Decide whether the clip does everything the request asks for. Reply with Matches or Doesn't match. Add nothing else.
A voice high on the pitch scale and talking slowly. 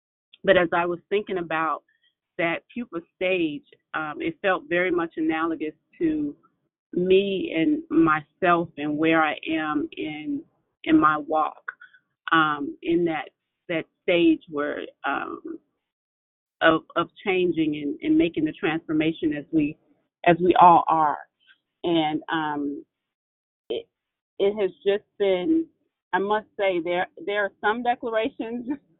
Matches